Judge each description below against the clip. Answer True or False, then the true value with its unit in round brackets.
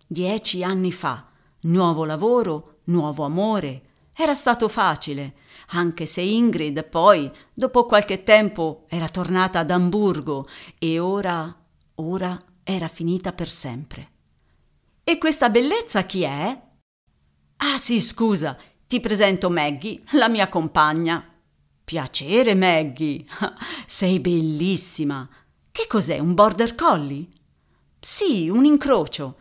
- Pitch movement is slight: False (5.3 semitones)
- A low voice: False (175 Hz)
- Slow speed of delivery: True (110 wpm)